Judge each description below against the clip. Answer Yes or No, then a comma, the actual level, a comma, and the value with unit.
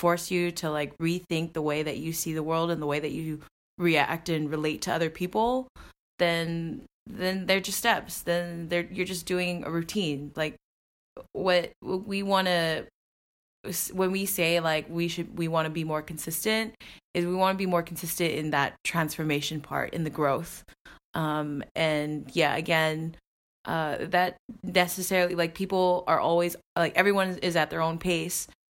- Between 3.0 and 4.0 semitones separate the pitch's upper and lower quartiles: No, narrow, 2.4 semitones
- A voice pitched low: No, medium, 170 Hz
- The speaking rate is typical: Yes, average, 175 wpm